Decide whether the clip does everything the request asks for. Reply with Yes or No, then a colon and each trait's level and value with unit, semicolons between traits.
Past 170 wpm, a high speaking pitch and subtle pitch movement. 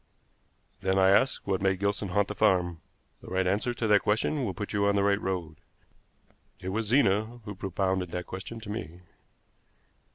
No: average, 185 wpm; low, 100 Hz; narrow, 1.9 semitones